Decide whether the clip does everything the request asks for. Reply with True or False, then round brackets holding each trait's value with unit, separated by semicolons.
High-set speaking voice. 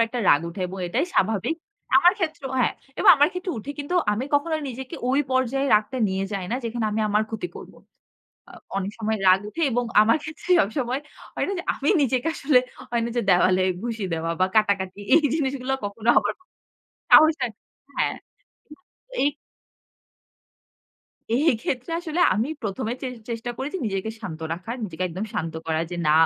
True (230 Hz)